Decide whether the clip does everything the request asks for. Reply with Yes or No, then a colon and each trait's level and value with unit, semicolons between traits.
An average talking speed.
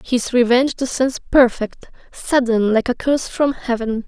Yes: average, 145 wpm